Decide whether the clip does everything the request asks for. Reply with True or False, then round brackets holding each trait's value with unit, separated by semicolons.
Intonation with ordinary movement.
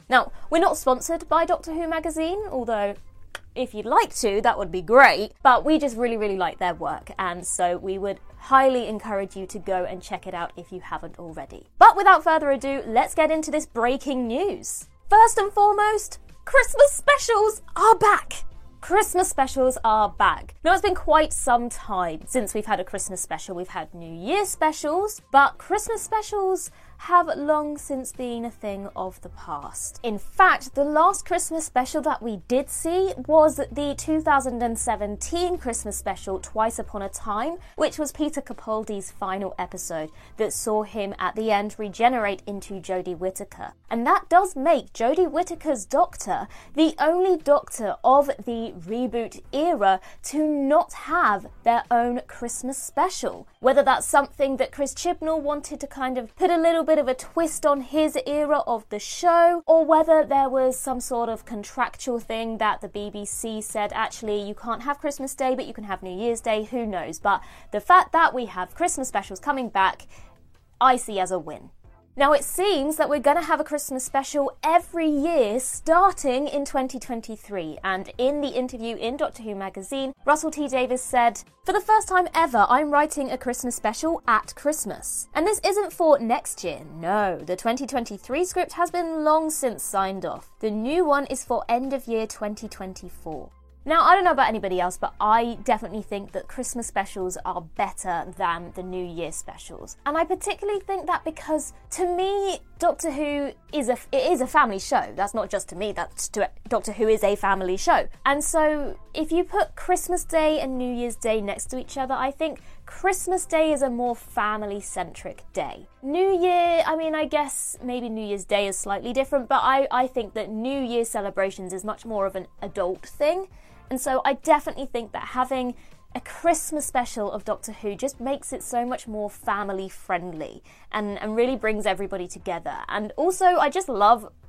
False (7.0 semitones)